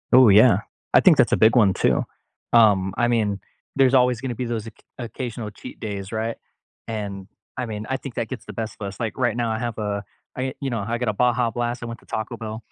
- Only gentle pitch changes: Yes, narrow, 2.3 semitones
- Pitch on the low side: Yes, low, 115 Hz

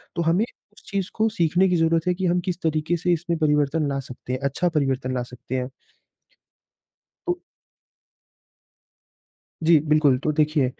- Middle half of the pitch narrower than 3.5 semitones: No, average, 4.2 semitones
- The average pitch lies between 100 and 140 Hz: No, medium, 160 Hz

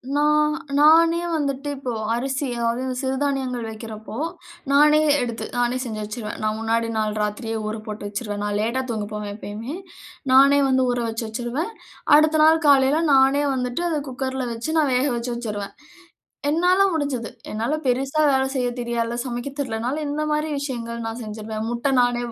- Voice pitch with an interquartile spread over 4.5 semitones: No, average, 3.9 semitones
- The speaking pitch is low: No, very high, 250 Hz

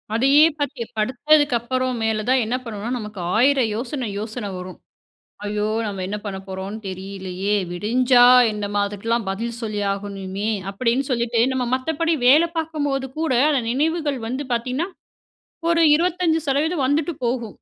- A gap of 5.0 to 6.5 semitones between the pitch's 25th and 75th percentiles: Yes, average, 5.3 semitones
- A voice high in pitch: Yes, high, 240 Hz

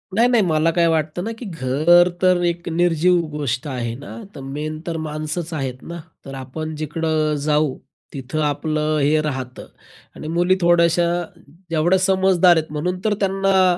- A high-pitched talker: No, medium, 160 Hz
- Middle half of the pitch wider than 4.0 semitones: No, average, 2.8 semitones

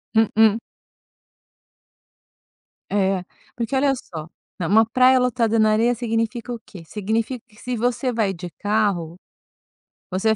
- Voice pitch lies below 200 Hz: No, high, 220 Hz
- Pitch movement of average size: Yes, average, 3.0 semitones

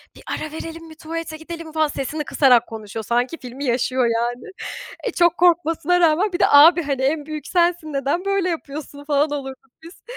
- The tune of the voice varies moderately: Yes, average, 3.6 semitones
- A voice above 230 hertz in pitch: Yes, very high, 310 Hz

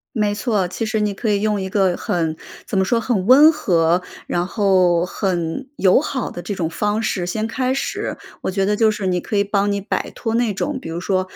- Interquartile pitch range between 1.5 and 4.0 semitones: Yes, average, 3.3 semitones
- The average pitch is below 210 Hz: Yes, high, 200 Hz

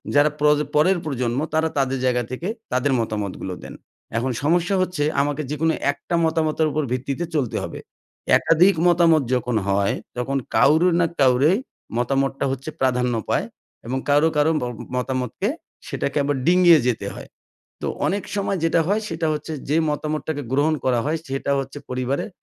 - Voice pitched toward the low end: No, medium, 145 Hz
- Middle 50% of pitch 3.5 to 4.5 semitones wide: Yes, average, 4.0 semitones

